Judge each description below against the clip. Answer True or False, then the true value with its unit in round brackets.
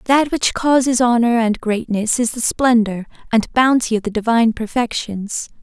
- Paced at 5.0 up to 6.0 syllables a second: False (4.7 syllables/s)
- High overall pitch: True (230 Hz)